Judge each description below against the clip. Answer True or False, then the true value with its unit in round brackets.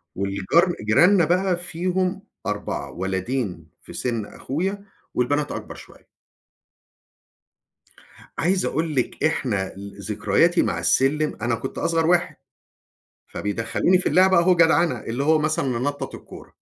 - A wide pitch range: True (8.6 semitones)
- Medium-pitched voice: True (145 Hz)